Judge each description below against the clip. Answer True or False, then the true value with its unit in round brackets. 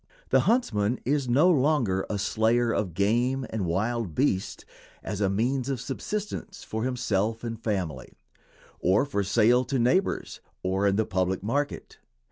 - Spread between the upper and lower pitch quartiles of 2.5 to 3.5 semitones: False (4.7 semitones)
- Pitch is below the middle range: True (115 Hz)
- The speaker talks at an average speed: True (150 wpm)